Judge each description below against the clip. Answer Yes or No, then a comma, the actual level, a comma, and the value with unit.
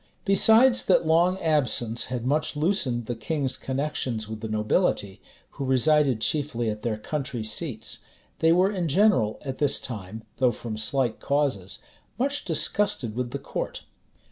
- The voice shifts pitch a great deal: Yes, wide, 6.3 semitones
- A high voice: No, low, 135 Hz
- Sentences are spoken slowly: No, average, 150 wpm